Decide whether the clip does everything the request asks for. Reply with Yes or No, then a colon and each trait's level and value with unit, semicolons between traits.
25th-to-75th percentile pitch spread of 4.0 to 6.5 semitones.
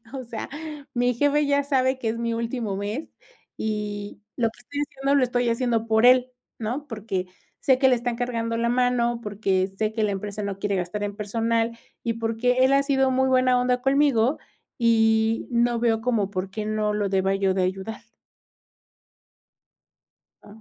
No: average, 3.0 semitones